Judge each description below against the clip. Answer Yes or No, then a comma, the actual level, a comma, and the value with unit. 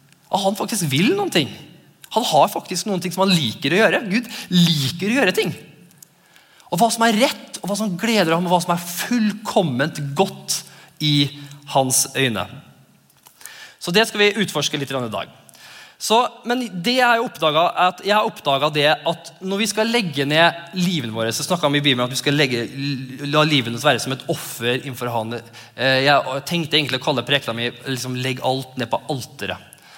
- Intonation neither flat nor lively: No, wide, 6.2 semitones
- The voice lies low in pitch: No, medium, 155 Hz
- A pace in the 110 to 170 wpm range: No, average, 185 wpm